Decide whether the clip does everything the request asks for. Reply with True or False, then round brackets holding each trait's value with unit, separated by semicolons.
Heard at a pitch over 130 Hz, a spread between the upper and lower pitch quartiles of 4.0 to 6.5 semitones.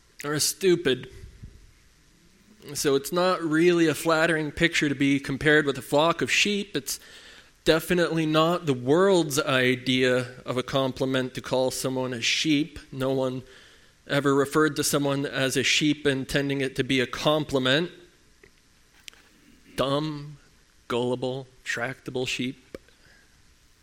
False (140 Hz; 3.3 semitones)